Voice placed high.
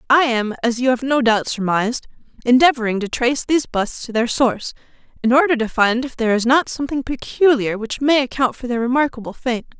Yes: high, 245 Hz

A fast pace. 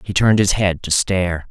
Yes: fast, 240 wpm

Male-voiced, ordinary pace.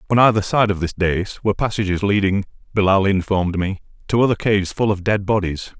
Yes: male; average, 195 wpm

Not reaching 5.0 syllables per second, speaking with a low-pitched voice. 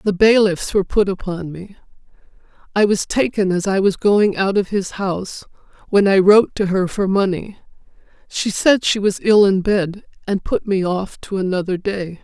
No: 4.8 syllables/s; high, 195 Hz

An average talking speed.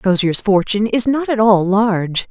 Yes: average, 180 wpm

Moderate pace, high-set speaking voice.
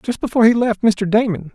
No: fast, 235 wpm; high, 220 Hz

